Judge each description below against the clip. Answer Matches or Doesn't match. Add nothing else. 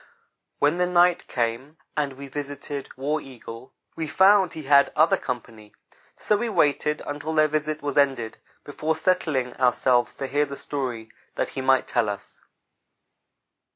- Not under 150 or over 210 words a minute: Matches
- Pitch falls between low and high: Matches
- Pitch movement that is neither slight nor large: Matches